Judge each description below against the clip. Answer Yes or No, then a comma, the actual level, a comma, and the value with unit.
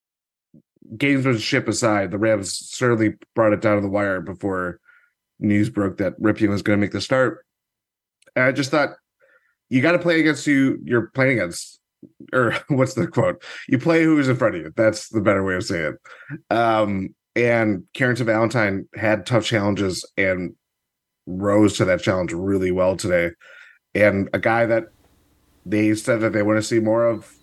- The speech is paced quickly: No, average, 185 wpm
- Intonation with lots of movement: No, average, 3.0 semitones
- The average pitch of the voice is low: Yes, low, 110 Hz